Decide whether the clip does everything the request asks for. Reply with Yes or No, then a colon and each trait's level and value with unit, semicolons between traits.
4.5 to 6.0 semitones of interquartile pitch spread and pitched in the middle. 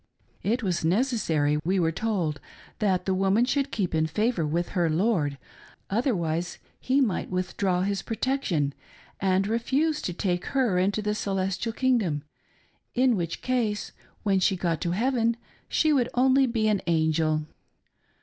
No: wide, 5.4 semitones; high, 195 Hz